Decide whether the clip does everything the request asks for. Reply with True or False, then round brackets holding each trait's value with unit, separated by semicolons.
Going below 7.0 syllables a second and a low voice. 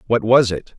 True (4.8 syllables/s; 115 Hz)